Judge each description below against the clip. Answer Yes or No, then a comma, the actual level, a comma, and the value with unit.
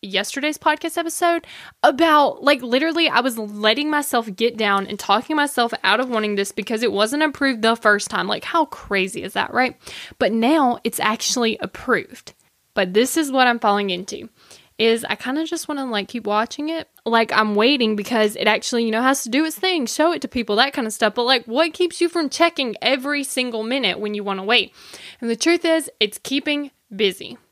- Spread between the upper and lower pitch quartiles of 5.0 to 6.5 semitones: Yes, wide, 5.6 semitones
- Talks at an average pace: No, fast, 215 wpm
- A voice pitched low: No, high, 245 Hz